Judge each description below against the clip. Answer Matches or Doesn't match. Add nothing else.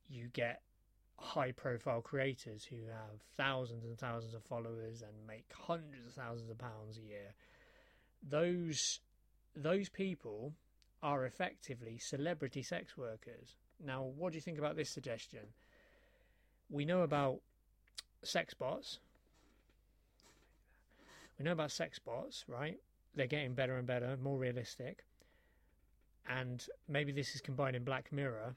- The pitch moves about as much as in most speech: Matches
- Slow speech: Matches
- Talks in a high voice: Doesn't match